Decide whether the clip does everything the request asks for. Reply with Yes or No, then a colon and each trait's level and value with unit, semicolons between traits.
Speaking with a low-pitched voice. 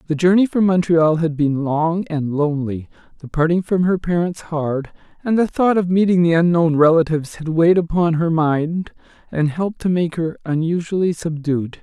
No: medium, 165 Hz